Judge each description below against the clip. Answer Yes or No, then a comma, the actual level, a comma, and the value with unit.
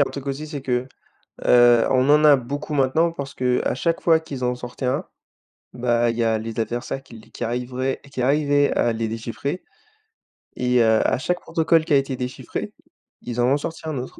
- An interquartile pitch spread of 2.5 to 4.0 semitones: Yes, average, 2.9 semitones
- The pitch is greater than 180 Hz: No, low, 130 Hz